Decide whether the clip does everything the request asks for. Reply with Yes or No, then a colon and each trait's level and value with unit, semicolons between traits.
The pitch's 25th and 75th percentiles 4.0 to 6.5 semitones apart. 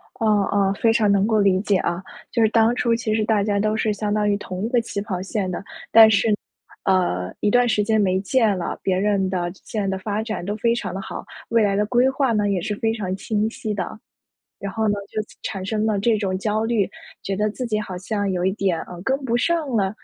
No: narrow, 2.4 semitones